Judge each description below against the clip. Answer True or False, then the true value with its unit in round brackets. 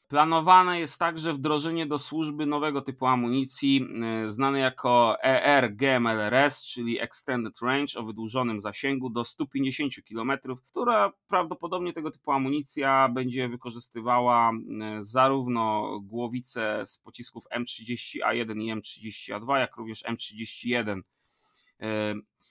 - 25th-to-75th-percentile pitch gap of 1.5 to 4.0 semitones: True (3.5 semitones)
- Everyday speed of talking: False (105 wpm)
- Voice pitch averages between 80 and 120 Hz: False (130 Hz)